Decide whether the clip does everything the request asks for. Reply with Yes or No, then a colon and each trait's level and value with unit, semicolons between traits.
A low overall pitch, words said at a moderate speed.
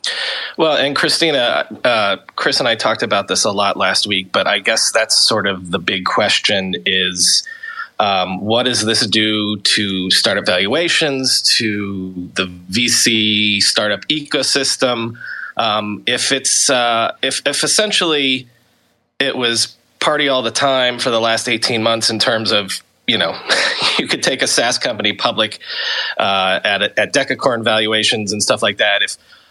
Yes: low, 115 Hz; average, 160 wpm